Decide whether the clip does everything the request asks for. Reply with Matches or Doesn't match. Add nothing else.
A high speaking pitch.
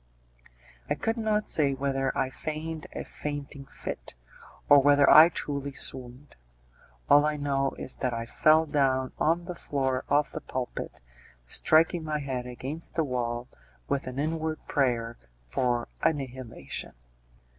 Doesn't match